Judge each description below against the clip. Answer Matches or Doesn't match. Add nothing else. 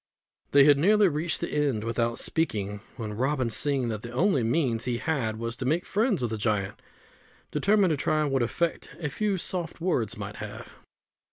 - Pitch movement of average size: Doesn't match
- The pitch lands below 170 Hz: Matches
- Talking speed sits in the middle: Matches